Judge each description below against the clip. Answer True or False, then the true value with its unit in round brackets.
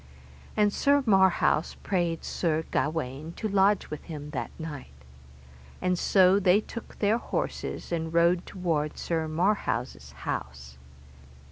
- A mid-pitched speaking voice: True (170 Hz)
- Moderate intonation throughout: True (4.2 semitones)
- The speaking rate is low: True (125 wpm)